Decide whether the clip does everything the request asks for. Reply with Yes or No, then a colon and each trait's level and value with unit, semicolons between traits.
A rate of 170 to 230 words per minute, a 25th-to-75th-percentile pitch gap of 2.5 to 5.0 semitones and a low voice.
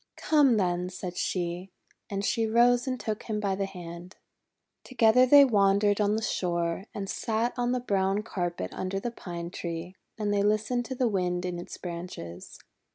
No: average, 175 wpm; average, 4.2 semitones; high, 200 Hz